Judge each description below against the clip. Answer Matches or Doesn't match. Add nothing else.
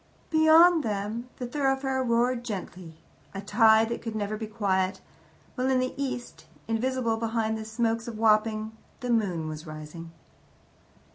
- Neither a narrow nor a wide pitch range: Matches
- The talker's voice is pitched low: Doesn't match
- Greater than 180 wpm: Doesn't match